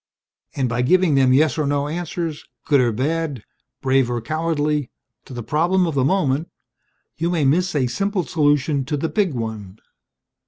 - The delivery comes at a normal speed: Yes, average, 170 wpm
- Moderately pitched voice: Yes, medium, 145 Hz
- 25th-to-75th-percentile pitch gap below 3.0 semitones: No, average, 4.0 semitones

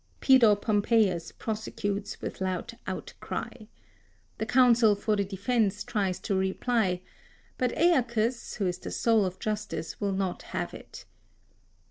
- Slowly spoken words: Yes, slow, 130 wpm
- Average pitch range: Yes, average, 3.4 semitones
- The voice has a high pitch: Yes, high, 210 Hz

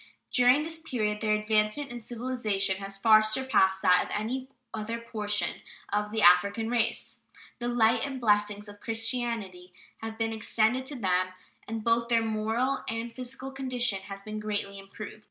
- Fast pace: No, average, 165 wpm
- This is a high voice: Yes, high, 220 Hz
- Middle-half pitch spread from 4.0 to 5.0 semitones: No, narrow, 2.6 semitones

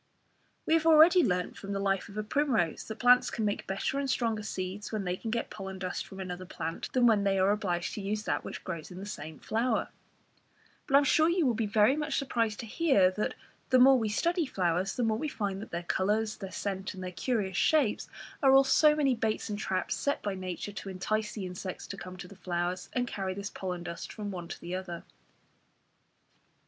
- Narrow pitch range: No, average, 4.6 semitones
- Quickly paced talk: Yes, fast, 225 wpm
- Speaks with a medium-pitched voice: No, high, 205 Hz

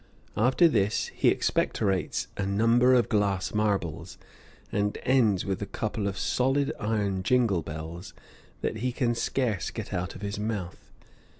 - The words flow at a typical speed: Yes, average, 145 wpm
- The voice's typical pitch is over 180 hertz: No, low, 105 Hz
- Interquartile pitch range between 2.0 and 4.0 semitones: Yes, average, 3.5 semitones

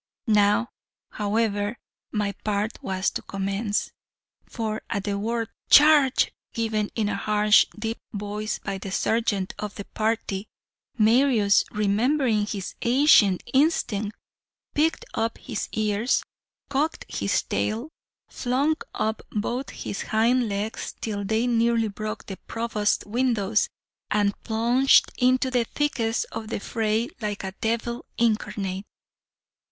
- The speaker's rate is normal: No, slow, 125 wpm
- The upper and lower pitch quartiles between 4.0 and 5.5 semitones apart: No, narrow, 2.4 semitones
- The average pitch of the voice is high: Yes, high, 220 Hz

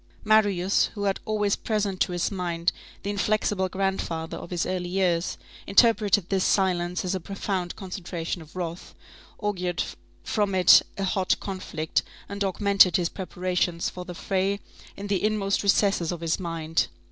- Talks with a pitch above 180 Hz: Yes, high, 190 Hz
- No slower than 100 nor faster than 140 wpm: No, average, 155 wpm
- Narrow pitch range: Yes, narrow, 2.3 semitones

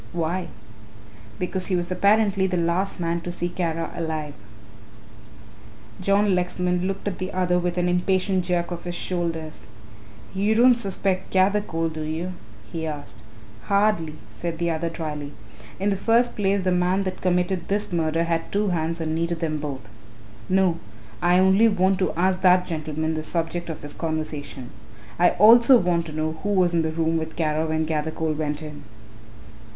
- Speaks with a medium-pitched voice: Yes, medium, 175 Hz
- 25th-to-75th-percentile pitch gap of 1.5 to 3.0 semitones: Yes, average, 2.7 semitones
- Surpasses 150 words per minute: Yes, average, 170 wpm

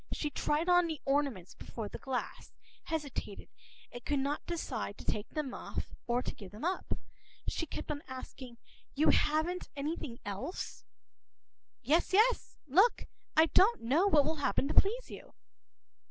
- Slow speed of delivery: No, average, 160 wpm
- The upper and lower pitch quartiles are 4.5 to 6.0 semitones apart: Yes, average, 4.8 semitones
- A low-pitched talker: No, very high, 295 Hz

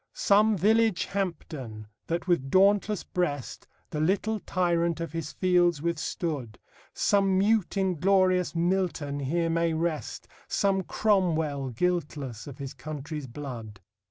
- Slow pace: Yes, slow, 120 wpm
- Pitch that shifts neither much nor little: Yes, average, 4.6 semitones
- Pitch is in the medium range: Yes, medium, 170 Hz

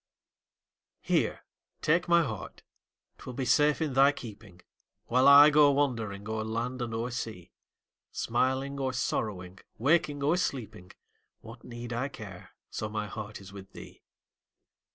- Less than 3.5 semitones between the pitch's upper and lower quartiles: No, average, 4.6 semitones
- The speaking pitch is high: No, low, 120 Hz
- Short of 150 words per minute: Yes, average, 140 wpm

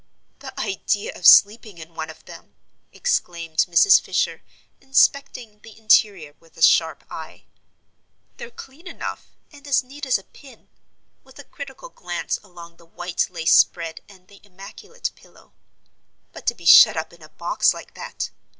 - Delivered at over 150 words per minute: Yes, average, 160 wpm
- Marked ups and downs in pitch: Yes, wide, 7.9 semitones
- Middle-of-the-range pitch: No, high, 195 Hz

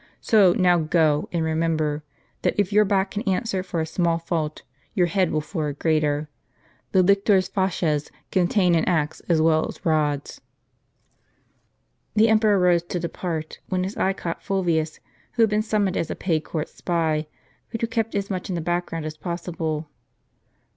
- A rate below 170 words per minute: No, average, 175 wpm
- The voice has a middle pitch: Yes, medium, 175 Hz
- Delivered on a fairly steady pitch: No, average, 3.4 semitones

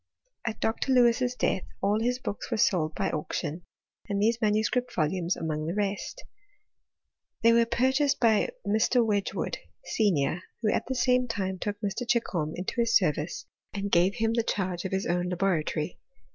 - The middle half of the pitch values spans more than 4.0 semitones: Yes, average, 4.5 semitones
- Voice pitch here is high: Yes, high, 205 Hz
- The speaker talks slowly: No, average, 175 wpm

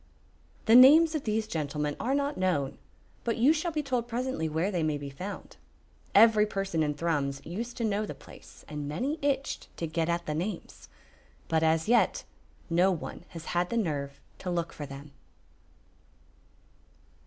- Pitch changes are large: Yes, wide, 7.1 semitones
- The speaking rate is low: No, average, 170 wpm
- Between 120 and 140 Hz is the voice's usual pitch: No, medium, 180 Hz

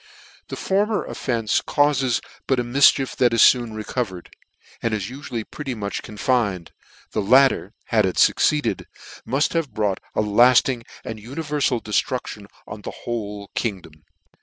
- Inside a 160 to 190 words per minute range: No, average, 145 wpm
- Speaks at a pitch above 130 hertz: No, low, 120 Hz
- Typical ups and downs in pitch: Yes, average, 4.2 semitones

